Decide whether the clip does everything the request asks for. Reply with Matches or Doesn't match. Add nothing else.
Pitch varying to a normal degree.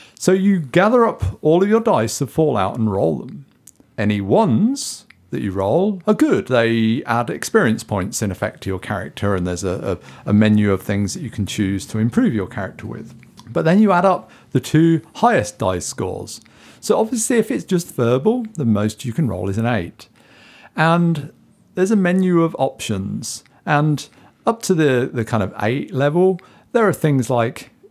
Doesn't match